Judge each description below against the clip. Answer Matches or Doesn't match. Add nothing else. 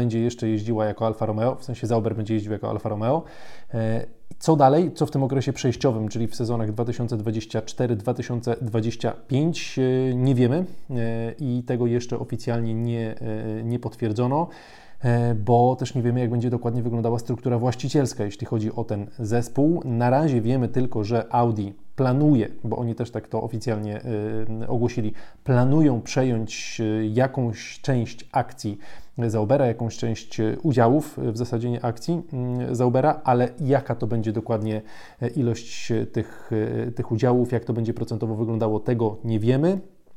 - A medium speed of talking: Matches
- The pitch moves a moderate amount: Doesn't match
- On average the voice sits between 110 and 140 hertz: Matches